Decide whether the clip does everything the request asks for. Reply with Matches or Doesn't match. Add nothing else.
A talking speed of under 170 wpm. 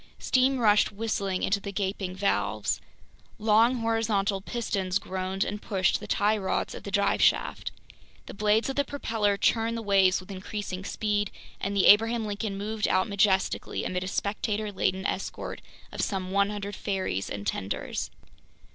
Matches